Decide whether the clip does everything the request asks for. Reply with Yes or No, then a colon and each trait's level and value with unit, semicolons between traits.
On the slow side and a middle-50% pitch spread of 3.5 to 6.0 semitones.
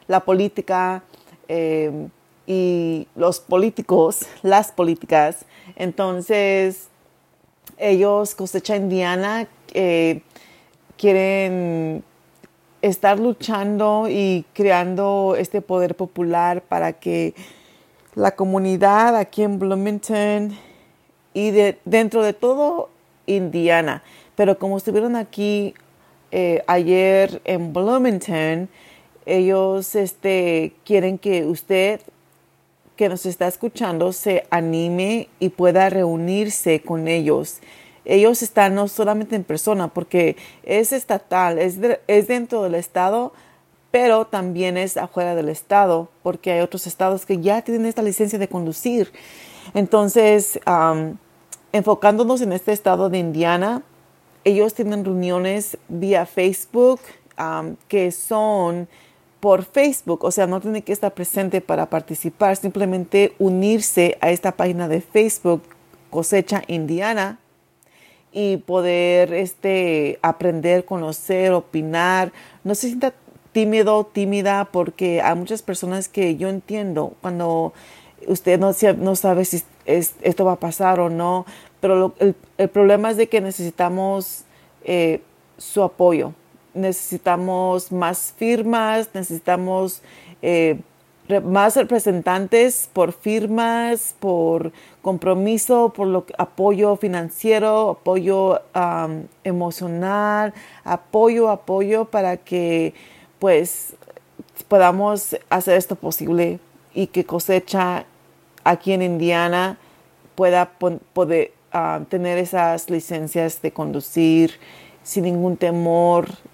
No: slow, 110 wpm; average, 2.9 semitones